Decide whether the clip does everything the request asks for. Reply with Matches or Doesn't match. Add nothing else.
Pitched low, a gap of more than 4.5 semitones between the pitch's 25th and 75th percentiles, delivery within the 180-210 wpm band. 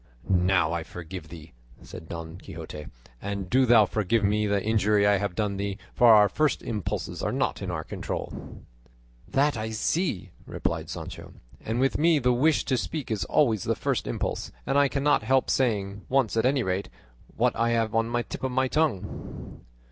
Matches